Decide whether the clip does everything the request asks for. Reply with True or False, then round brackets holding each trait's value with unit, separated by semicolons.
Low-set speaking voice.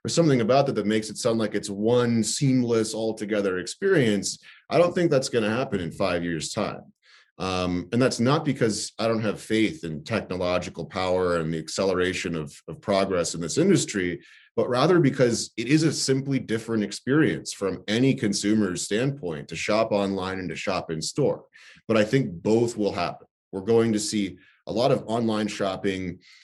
True (105 Hz)